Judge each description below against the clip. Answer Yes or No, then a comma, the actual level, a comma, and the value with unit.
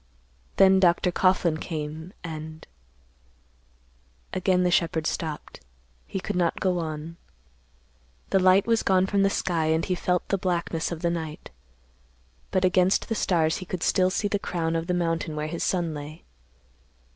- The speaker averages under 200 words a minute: Yes, average, 160 wpm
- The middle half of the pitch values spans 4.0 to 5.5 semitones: No, narrow, 2.4 semitones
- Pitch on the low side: No, medium, 175 Hz